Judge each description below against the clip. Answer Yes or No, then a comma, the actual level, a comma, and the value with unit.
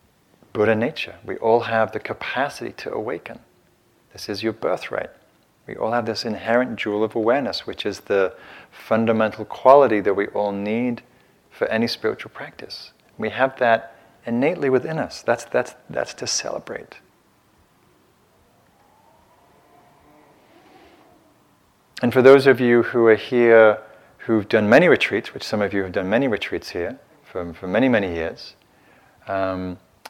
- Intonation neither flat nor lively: No, narrow, 2.0 semitones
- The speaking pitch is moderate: No, low, 110 Hz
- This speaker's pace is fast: No, average, 145 wpm